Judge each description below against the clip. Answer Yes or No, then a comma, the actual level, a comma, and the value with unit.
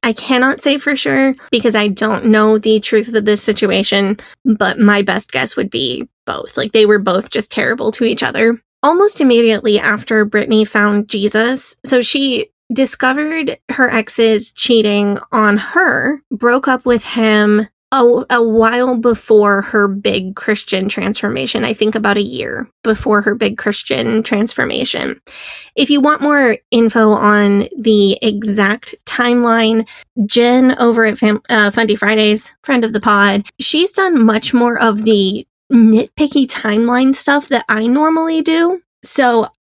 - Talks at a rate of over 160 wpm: No, average, 150 wpm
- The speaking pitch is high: Yes, high, 225 Hz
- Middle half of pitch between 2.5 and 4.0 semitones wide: Yes, average, 3.0 semitones